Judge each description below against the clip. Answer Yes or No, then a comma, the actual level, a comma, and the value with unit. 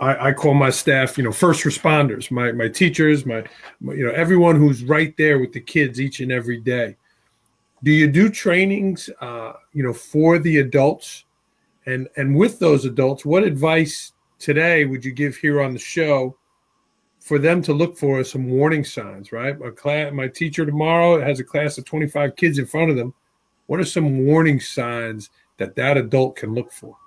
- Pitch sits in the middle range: Yes, medium, 145 Hz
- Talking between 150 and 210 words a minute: Yes, average, 195 wpm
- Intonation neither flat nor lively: Yes, average, 3.5 semitones